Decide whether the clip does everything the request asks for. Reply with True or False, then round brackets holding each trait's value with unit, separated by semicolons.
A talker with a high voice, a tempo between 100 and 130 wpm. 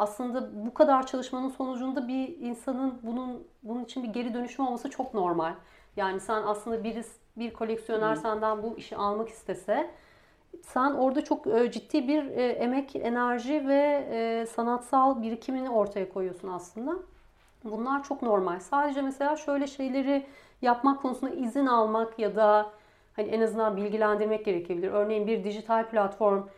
False (235 Hz; 140 wpm)